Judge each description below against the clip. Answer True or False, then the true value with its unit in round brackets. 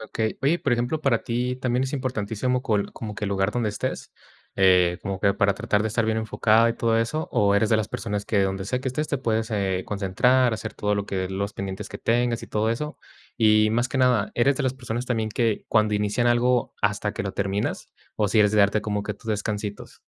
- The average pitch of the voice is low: True (110 Hz)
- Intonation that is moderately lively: True (3.0 semitones)